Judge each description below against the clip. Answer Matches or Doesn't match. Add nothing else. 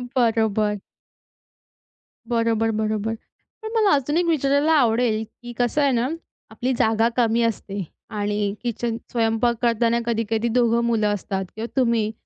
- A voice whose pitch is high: Matches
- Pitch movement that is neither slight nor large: Doesn't match